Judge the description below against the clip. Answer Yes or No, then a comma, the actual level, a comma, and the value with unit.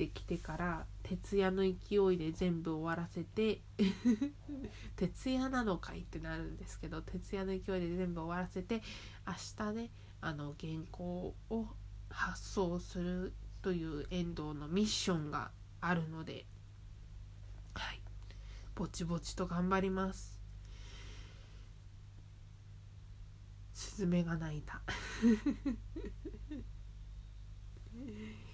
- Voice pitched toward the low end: No, medium, 160 Hz